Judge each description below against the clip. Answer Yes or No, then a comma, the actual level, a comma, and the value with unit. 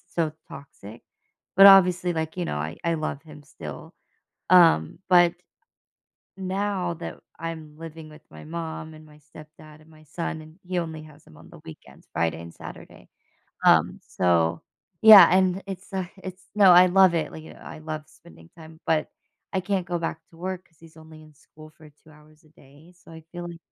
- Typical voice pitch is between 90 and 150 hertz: No, medium, 160 Hz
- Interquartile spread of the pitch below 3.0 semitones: Yes, narrow, 2.6 semitones